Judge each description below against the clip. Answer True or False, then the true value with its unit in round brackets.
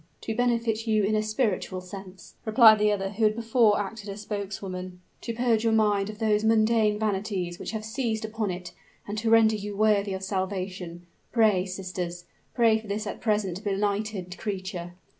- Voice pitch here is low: False (210 Hz)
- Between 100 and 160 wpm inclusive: False (180 wpm)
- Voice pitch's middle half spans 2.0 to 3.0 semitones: True (2.5 semitones)